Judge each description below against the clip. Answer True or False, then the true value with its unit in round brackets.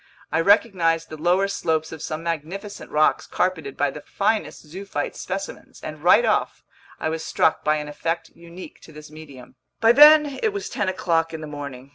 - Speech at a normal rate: True (185 wpm)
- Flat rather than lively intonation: False (4.4 semitones)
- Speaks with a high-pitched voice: False (165 Hz)